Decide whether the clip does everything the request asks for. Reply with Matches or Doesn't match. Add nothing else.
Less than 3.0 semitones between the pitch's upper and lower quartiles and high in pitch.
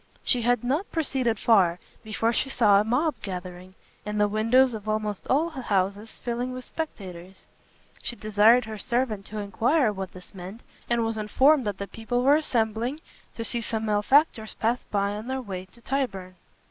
Doesn't match